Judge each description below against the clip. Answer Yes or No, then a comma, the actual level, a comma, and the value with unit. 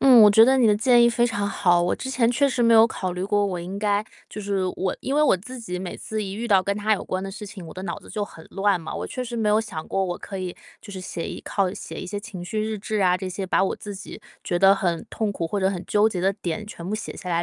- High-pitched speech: Yes, high, 200 Hz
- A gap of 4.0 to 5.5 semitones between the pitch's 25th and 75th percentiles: No, average, 2.9 semitones